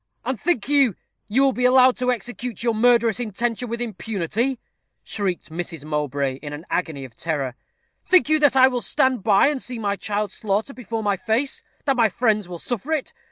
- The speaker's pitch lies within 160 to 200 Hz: No, high, 225 Hz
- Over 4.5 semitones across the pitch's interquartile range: Yes, average, 5.3 semitones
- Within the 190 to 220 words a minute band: Yes, average, 195 wpm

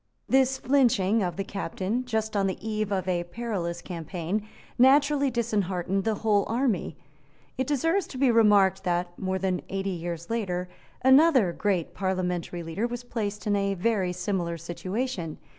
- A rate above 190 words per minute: No, average, 155 wpm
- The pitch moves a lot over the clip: No, average, 4.6 semitones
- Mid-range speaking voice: No, high, 200 Hz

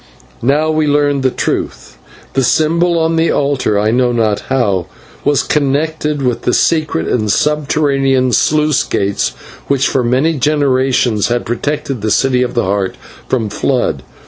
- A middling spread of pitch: Yes, average, 3.9 semitones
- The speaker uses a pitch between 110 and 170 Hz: Yes, low, 135 Hz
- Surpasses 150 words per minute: No, average, 145 wpm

